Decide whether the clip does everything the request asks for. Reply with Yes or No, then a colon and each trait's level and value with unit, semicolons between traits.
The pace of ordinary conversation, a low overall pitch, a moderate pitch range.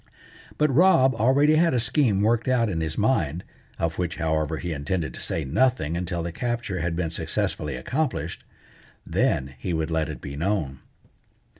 No: average, 170 wpm; very low, 90 Hz; wide, 7.6 semitones